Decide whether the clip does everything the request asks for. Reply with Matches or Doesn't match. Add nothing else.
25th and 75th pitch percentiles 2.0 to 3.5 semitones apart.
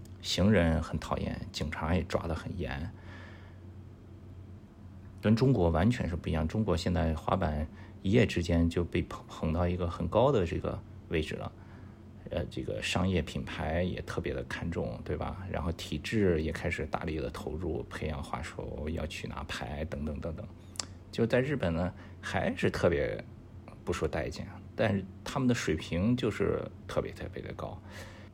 Matches